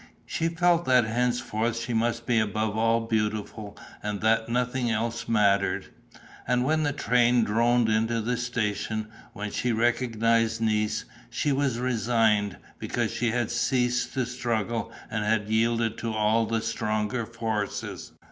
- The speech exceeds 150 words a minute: No, average, 145 wpm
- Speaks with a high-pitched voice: No, low, 115 Hz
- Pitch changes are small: Yes, narrow, 2.0 semitones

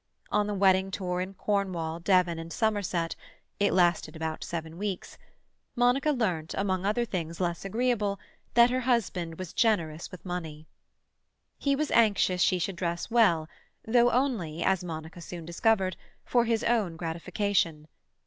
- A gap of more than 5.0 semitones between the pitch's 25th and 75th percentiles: No, average, 4.6 semitones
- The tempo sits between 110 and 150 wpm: Yes, average, 140 wpm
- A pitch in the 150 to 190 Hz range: Yes, medium, 185 Hz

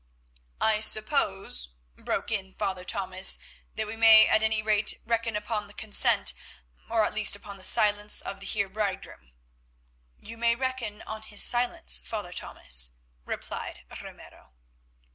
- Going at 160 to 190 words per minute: No, average, 145 wpm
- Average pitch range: No, narrow, 2.3 semitones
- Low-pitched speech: No, high, 210 Hz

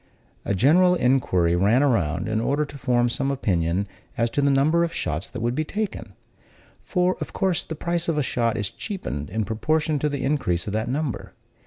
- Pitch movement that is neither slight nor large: No, wide, 6.2 semitones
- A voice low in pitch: Yes, low, 130 Hz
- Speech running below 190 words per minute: No, average, 200 wpm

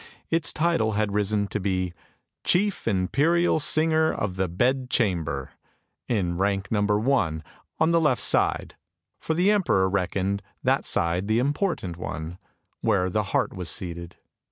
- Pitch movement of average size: No, wide, 7.8 semitones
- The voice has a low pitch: Yes, low, 105 Hz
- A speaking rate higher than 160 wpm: No, average, 155 wpm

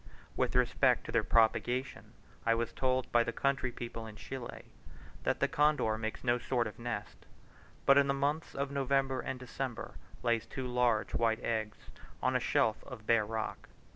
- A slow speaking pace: No, average, 175 wpm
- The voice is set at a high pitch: No, low, 120 Hz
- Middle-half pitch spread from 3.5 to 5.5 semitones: No, average, 2.7 semitones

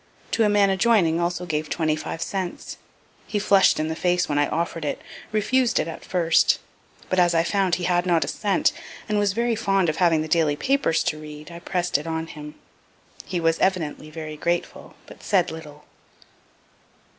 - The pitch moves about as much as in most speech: Yes, average, 3.4 semitones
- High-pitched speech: No, medium, 170 Hz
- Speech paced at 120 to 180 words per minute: No, average, 190 wpm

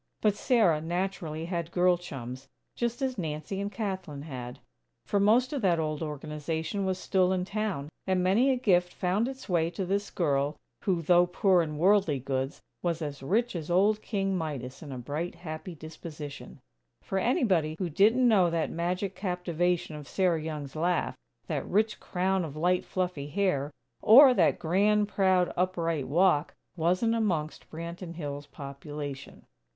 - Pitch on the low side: No, medium, 175 Hz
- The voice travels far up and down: No, average, 4.1 semitones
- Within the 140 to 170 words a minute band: Yes, average, 160 wpm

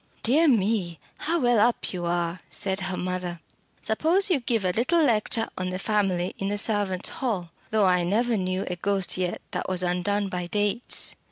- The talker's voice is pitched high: Yes, high, 195 Hz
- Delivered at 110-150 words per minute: No, average, 185 wpm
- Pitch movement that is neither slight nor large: Yes, average, 3.8 semitones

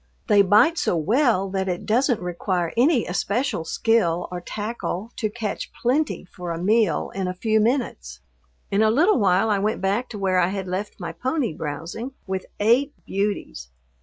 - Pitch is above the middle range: Yes, high, 205 Hz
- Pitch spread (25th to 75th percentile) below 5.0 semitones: Yes, average, 4.5 semitones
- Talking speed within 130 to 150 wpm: No, average, 175 wpm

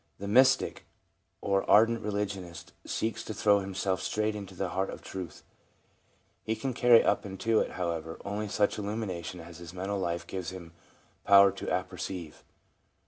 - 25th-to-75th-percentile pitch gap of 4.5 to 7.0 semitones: No, average, 2.8 semitones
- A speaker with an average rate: Yes, average, 155 wpm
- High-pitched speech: No, very low, 95 Hz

